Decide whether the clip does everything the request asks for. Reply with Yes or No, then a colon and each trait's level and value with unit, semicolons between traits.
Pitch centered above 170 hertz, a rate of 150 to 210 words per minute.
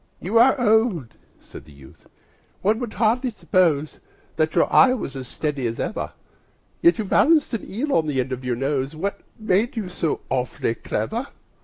Yes: medium, 185 Hz; average, 180 wpm